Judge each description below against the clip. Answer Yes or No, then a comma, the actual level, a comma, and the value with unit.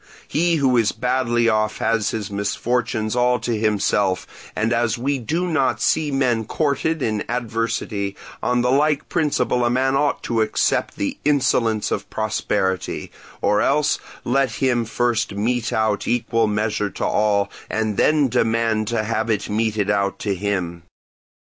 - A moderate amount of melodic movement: Yes, average, 3.2 semitones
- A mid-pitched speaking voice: No, low, 115 Hz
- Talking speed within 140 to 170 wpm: Yes, average, 155 wpm